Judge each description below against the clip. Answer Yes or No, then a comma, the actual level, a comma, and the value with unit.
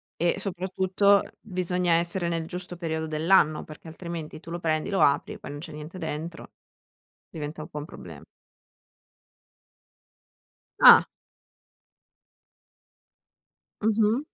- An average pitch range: Yes, average, 3.0 semitones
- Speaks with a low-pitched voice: No, medium, 170 Hz